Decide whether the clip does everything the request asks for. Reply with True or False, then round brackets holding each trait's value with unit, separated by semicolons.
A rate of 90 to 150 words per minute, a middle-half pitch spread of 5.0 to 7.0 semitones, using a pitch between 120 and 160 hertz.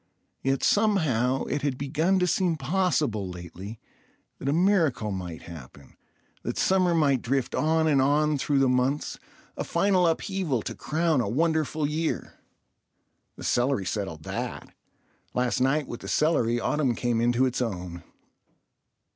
True (140 wpm; 5.4 semitones; 135 Hz)